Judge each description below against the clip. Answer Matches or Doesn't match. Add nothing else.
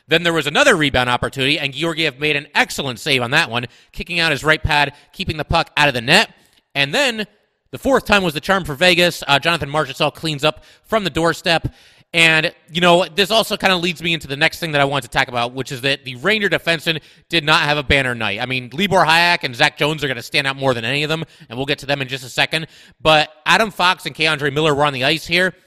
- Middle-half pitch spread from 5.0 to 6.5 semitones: Doesn't match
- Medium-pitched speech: Matches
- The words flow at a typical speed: Doesn't match